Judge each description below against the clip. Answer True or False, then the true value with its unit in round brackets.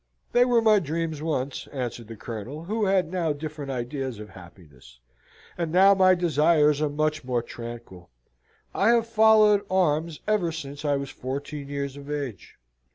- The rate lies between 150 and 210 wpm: True (160 wpm)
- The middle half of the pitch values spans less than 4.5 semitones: False (5.6 semitones)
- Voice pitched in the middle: True (150 Hz)